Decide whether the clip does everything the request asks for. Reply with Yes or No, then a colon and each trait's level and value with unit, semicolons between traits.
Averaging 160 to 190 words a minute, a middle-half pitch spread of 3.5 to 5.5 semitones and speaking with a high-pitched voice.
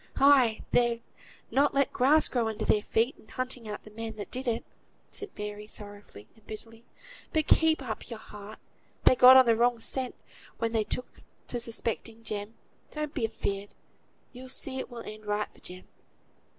No: average, 180 wpm; average, 3.1 semitones; high, 230 Hz